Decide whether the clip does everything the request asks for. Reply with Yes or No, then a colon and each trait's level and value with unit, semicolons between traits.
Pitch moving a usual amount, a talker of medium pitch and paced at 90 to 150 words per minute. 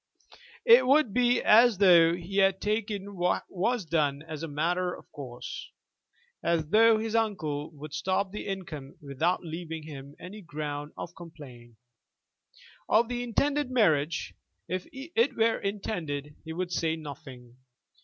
No: wide, 6.0 semitones; medium, 175 Hz; average, 145 wpm